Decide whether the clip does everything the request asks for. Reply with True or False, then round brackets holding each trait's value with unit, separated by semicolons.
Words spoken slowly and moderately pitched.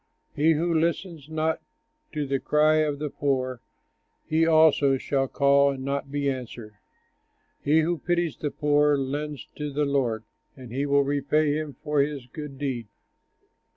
False (155 wpm; 145 Hz)